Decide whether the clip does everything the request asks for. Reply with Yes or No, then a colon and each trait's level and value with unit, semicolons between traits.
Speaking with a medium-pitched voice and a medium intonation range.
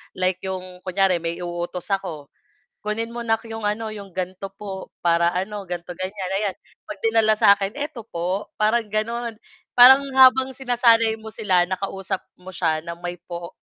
No: high, 195 Hz; average, 3.6 semitones